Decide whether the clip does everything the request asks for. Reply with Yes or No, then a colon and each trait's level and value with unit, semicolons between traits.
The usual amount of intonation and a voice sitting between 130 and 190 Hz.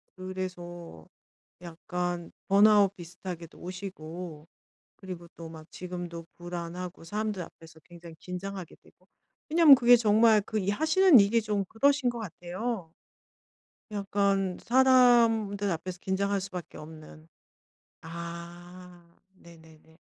Yes: average, 3.4 semitones; medium, 185 Hz